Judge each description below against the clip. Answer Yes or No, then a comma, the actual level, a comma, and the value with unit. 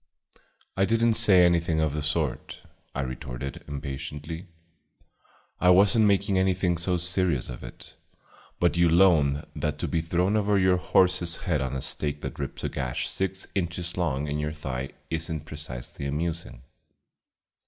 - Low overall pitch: Yes, very low, 85 Hz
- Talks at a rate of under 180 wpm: Yes, average, 165 wpm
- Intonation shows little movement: No, average, 4.1 semitones